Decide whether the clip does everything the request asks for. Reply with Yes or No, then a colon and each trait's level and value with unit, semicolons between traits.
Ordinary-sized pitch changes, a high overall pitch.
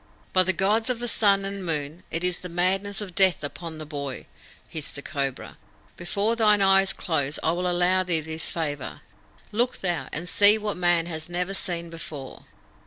No: average, 3.6 semitones; medium, 175 Hz